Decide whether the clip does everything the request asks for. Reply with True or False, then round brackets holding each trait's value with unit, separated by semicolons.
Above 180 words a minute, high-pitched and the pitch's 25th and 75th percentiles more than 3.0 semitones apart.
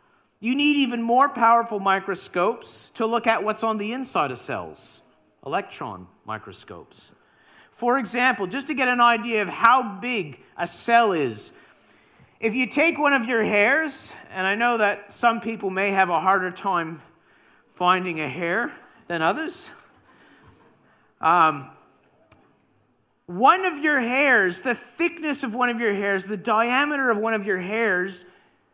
False (150 wpm; 230 Hz; 4.8 semitones)